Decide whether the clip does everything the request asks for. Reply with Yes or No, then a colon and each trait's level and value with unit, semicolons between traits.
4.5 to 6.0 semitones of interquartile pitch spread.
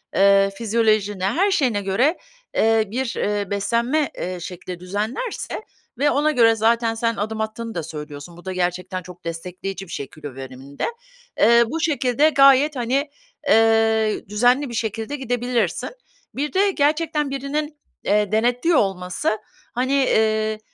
Yes: wide, 5.5 semitones